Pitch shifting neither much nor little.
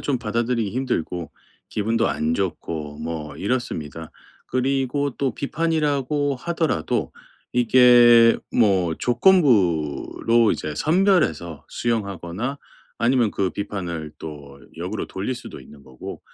No: wide, 7.6 semitones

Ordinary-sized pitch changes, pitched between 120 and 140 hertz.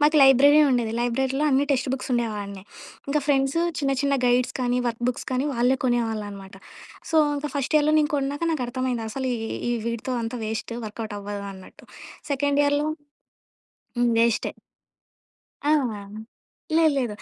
No: average, 3.4 semitones; very high, 255 Hz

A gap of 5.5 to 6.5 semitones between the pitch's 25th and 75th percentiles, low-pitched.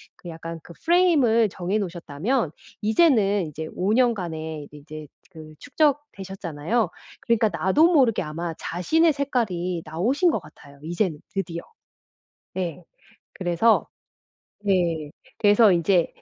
No: wide, 5.9 semitones; medium, 185 Hz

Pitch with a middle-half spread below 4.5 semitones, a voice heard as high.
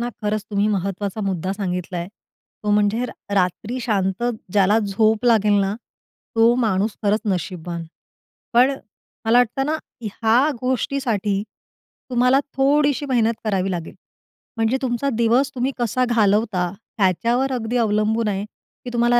Yes: average, 3.4 semitones; high, 220 Hz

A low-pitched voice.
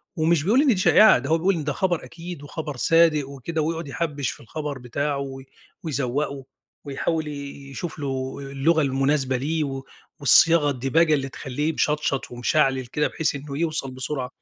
No: medium, 145 Hz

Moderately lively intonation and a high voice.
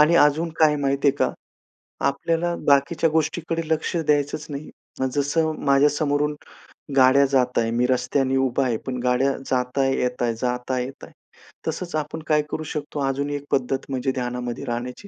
No: average, 3.0 semitones; medium, 140 Hz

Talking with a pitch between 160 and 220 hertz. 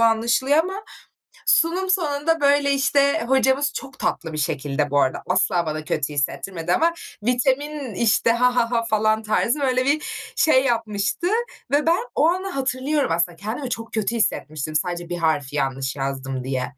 No: high, 230 Hz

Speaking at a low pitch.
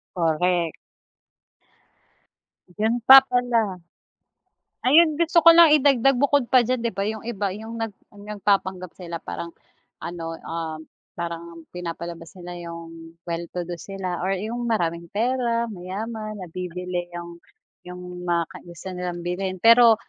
No: medium, 185 Hz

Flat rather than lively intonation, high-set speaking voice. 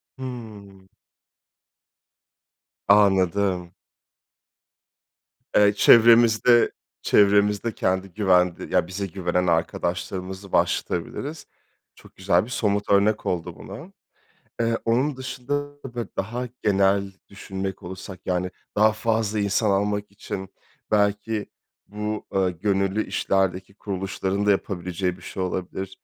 No: narrow, 2.3 semitones; low, 100 Hz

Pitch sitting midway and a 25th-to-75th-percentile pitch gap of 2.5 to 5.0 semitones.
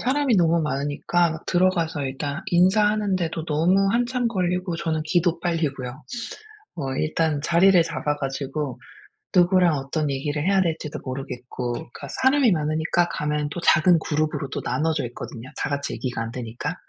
Yes: medium, 160 Hz; average, 4.1 semitones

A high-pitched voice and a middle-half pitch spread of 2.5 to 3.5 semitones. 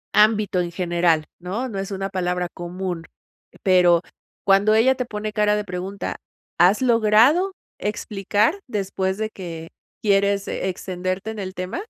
Yes: high, 195 Hz; average, 2.9 semitones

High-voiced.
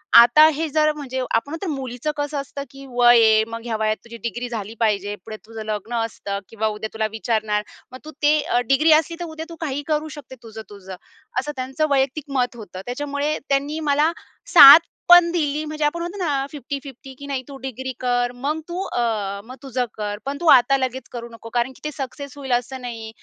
Yes: very high, 260 Hz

